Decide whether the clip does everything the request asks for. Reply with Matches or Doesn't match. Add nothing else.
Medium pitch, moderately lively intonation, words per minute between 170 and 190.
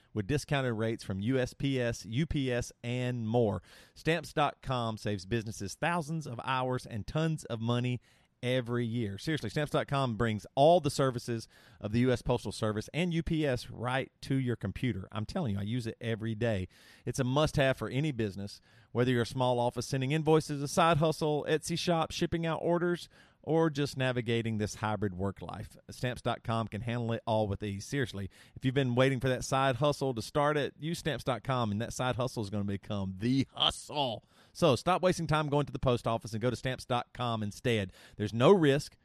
Doesn't match